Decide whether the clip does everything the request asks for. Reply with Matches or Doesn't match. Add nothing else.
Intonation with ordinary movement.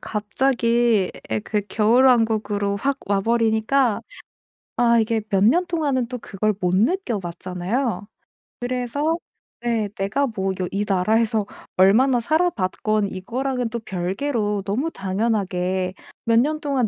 Matches